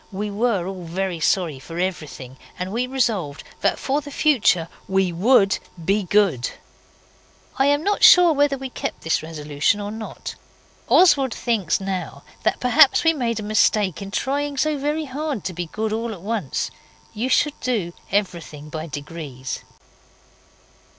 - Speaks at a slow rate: No, average, 155 wpm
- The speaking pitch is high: Yes, high, 205 Hz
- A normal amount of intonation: No, wide, 7.4 semitones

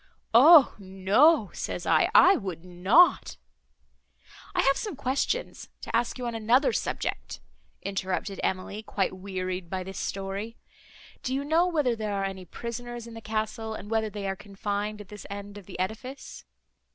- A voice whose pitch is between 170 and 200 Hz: No, high, 210 Hz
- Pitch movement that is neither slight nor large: Yes, average, 3.9 semitones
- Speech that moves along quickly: No, average, 165 wpm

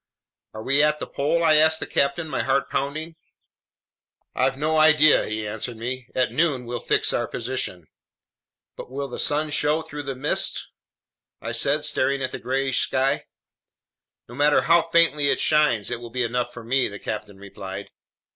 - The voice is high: No, low, 135 Hz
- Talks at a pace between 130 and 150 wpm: No, average, 175 wpm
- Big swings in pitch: No, average, 3.9 semitones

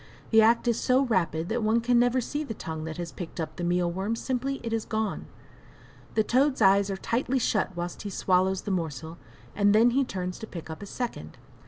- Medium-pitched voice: No, high, 210 Hz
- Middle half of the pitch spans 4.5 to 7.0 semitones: Yes, average, 5.2 semitones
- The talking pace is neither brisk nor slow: No, fast, 220 wpm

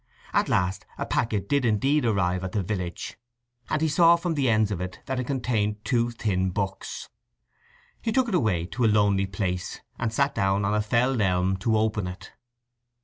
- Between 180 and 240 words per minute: Yes, average, 195 wpm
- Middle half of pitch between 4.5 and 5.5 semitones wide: Yes, average, 4.8 semitones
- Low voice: Yes, low, 105 Hz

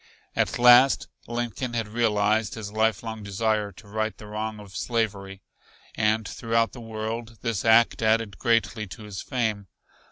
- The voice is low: Yes, low, 110 Hz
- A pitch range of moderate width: No, narrow, 1.7 semitones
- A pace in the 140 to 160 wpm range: Yes, average, 150 wpm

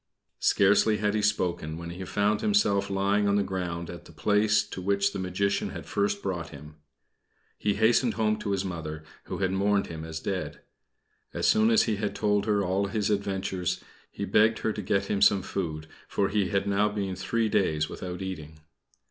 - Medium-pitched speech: No, low, 100 Hz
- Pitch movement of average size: No, narrow, 2.3 semitones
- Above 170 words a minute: Yes, average, 195 wpm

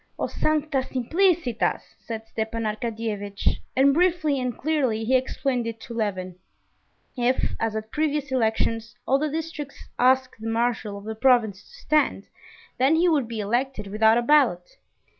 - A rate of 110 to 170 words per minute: Yes, average, 155 wpm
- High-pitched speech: Yes, high, 245 Hz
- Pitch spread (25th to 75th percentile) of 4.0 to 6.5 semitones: Yes, average, 4.3 semitones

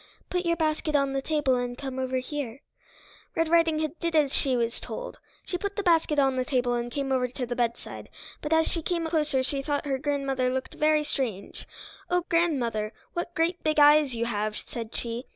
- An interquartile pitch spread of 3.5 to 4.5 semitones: Yes, average, 4.1 semitones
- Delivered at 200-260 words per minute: Yes, fast, 205 wpm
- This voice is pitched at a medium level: No, very high, 280 Hz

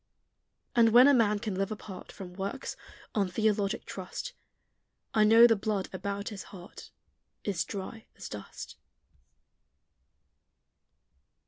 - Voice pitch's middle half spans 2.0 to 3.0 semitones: Yes, narrow, 2.4 semitones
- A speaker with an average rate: No, slow, 120 wpm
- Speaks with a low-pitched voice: No, high, 205 Hz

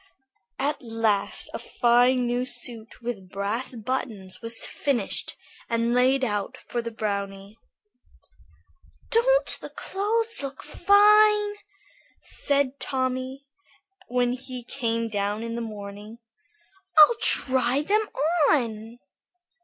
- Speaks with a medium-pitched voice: No, high, 245 Hz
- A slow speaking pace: Yes, slow, 105 wpm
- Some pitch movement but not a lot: Yes, average, 3.7 semitones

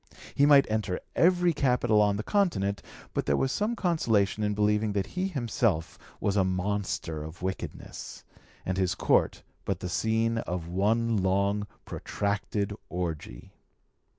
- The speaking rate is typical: Yes, average, 145 wpm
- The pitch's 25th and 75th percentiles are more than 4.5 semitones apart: No, average, 3.7 semitones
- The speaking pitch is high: No, low, 105 Hz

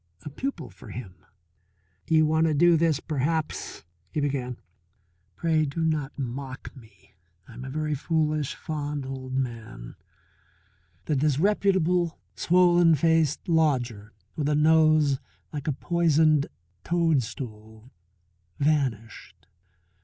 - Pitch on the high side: No, medium, 150 Hz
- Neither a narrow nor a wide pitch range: Yes, average, 4.0 semitones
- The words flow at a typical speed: No, slow, 115 wpm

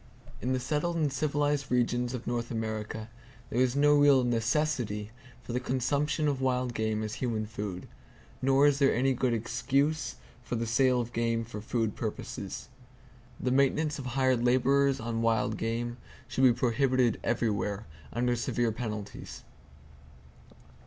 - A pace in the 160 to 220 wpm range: No, average, 150 wpm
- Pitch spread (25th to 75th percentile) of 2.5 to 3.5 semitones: Yes, average, 2.9 semitones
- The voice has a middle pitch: No, low, 125 Hz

